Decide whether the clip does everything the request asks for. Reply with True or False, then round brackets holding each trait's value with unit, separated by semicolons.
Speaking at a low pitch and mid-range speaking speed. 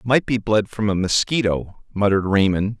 True (105 Hz; 170 wpm)